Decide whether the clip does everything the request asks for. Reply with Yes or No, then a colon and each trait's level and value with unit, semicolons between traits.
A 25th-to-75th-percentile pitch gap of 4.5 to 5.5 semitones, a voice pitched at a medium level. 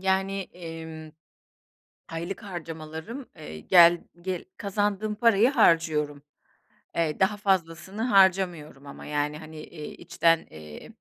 No: average, 3.8 semitones; medium, 170 Hz